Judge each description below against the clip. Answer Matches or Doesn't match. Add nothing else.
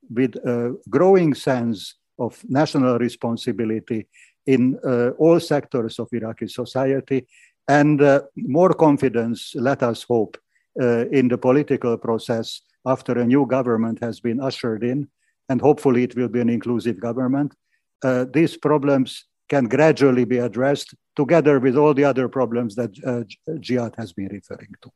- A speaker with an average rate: Matches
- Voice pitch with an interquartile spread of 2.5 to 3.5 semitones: Matches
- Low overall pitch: Matches